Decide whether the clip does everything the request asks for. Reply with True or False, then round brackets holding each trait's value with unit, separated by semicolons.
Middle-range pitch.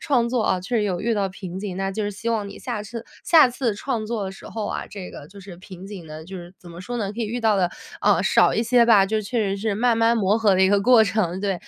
False (205 Hz)